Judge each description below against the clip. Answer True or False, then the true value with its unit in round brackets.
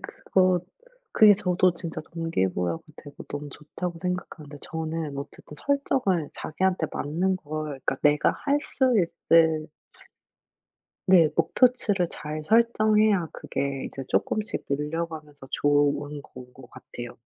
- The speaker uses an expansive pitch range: False (4.3 semitones)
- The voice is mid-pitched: True (160 Hz)